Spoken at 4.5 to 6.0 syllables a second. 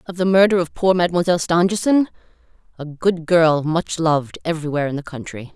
No: 6.2 syllables/s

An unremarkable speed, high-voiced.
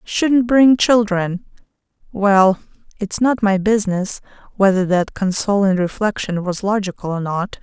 No: slow, 125 wpm; high, 200 Hz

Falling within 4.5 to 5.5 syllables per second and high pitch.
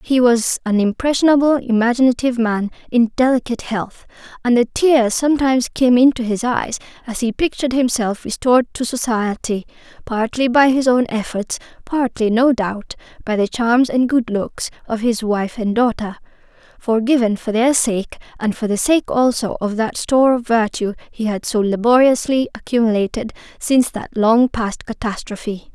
Yes: 5.0 syllables/s; high, 235 Hz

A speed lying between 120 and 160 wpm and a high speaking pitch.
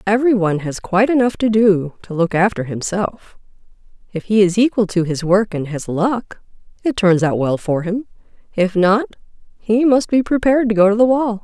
No: average, 200 wpm; high, 205 Hz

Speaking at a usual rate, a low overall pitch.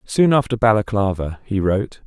Yes: average, 145 wpm; low, 105 Hz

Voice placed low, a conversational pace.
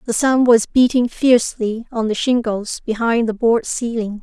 No: high, 230 Hz; average, 170 wpm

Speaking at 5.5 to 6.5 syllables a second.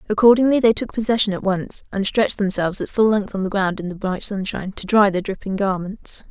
Yes: 6.0 syllables/s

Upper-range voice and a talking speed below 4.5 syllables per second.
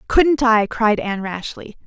Yes: high, 230 Hz; 4.3 syllables/s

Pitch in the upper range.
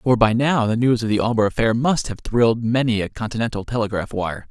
No: low, 115 Hz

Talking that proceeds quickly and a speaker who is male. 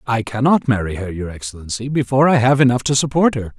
Yes: fast, 215 wpm; male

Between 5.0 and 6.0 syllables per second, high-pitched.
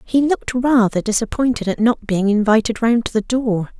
Yes: 5.2 syllables/s; high, 230 Hz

